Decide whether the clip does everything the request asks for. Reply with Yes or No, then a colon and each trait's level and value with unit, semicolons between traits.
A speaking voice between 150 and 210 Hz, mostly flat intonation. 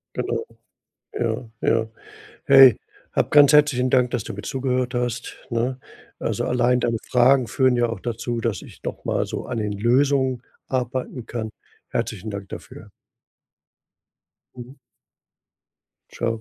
No: low, 125 Hz; narrow, 2.1 semitones